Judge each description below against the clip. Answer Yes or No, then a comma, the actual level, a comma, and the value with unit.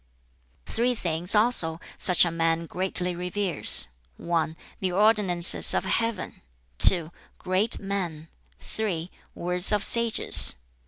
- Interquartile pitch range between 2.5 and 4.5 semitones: Yes, average, 3.7 semitones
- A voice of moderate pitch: Yes, medium, 180 Hz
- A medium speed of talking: No, slow, 110 wpm